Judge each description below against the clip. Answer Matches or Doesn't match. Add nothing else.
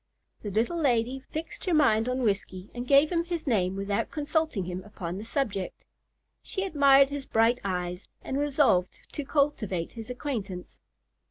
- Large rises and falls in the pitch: Matches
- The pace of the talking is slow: Doesn't match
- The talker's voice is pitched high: Matches